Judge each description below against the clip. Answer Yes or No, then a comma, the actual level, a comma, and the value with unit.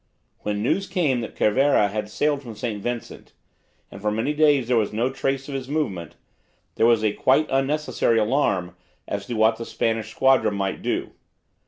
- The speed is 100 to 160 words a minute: No, average, 180 wpm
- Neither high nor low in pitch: No, low, 115 Hz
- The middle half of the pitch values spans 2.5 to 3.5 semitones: No, average, 4.3 semitones